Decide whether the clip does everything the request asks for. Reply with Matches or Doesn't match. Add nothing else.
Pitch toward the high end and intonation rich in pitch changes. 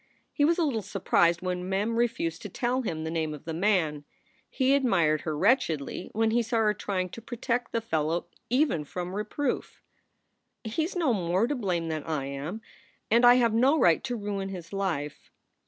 Matches